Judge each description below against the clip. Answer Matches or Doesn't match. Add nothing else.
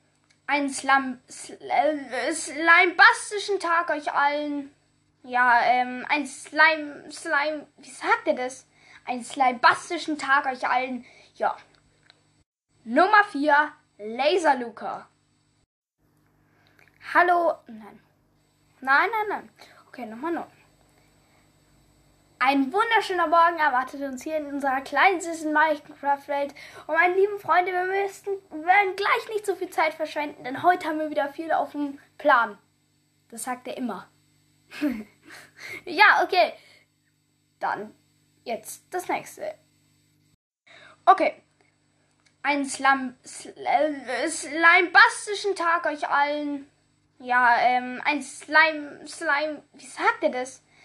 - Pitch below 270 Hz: Doesn't match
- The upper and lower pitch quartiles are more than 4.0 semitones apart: Matches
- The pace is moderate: Doesn't match